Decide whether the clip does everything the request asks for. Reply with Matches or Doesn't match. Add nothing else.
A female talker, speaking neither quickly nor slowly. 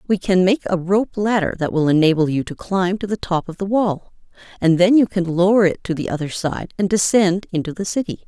Doesn't match